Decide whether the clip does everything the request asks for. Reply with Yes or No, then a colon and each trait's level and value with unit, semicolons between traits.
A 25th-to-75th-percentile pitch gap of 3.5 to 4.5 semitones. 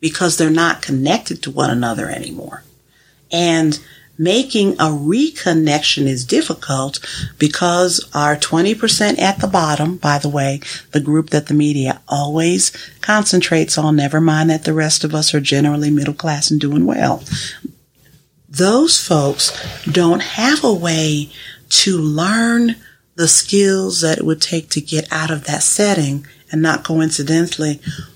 No: average, 3.1 semitones